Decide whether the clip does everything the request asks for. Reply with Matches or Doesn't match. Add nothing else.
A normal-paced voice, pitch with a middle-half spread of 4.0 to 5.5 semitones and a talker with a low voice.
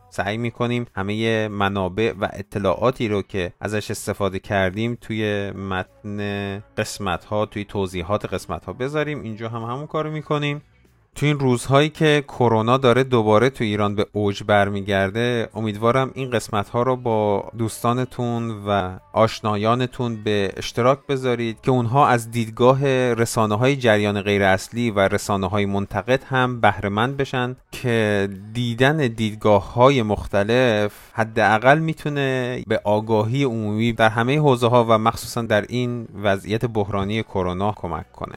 Doesn't match